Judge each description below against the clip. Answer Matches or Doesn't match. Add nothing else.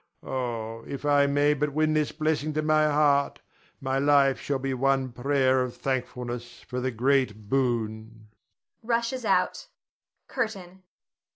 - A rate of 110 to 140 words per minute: Matches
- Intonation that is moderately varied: Matches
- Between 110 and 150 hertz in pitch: Matches